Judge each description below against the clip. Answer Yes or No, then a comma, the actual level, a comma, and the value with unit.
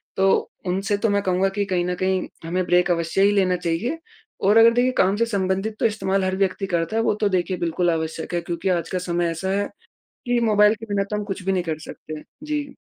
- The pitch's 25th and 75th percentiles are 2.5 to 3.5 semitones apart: Yes, average, 2.8 semitones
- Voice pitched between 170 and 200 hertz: Yes, high, 190 Hz